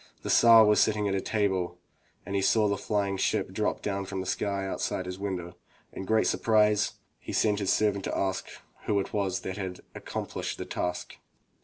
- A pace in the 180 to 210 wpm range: Yes, average, 200 wpm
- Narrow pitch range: Yes, narrow, 1.9 semitones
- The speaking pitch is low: Yes, low, 100 Hz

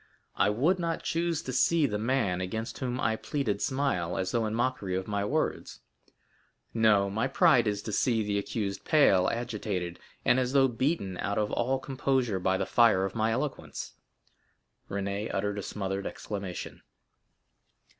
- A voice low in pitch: Yes, low, 110 Hz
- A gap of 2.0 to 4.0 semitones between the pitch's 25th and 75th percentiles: No, average, 4.7 semitones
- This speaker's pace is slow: No, average, 165 wpm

